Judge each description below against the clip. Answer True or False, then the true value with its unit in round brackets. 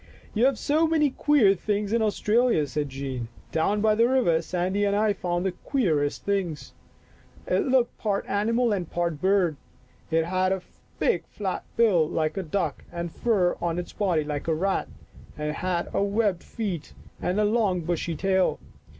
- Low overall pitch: False (190 Hz)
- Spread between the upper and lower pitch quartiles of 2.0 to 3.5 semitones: False (4.0 semitones)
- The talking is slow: False (185 wpm)